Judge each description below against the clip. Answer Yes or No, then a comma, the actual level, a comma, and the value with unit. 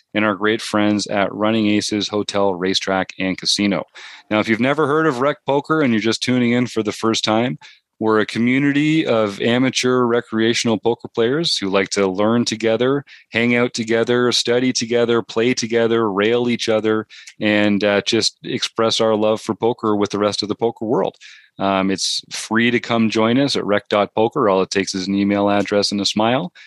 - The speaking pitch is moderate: No, low, 110 Hz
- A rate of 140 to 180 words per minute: No, average, 190 wpm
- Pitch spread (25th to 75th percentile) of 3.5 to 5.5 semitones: No, narrow, 2.6 semitones